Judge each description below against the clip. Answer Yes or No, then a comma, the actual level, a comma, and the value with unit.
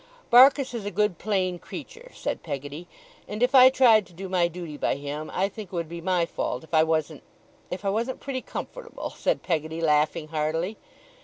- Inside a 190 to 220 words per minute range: Yes, average, 200 wpm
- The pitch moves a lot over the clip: Yes, wide, 5.7 semitones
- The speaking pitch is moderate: Yes, medium, 180 Hz